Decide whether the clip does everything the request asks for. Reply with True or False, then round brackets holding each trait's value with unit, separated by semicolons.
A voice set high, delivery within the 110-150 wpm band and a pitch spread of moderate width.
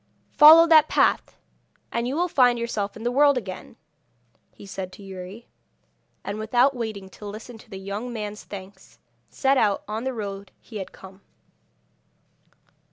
False (220 Hz; 160 wpm; 3.9 semitones)